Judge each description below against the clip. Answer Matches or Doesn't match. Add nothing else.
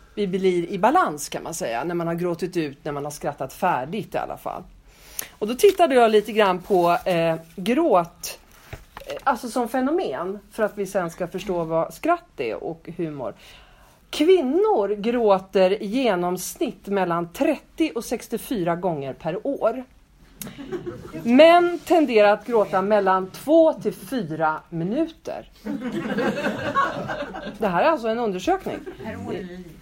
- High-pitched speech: Matches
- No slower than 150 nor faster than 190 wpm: Doesn't match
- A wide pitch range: Matches